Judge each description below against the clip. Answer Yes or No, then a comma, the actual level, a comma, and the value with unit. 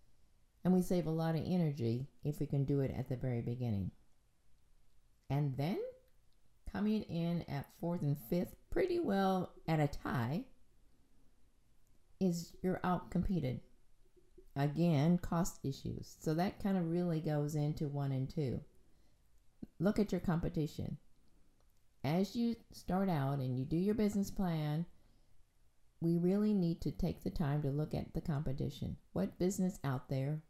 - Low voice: No, medium, 165 Hz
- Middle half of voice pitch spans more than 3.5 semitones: Yes, average, 4.6 semitones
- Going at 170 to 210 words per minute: No, average, 150 wpm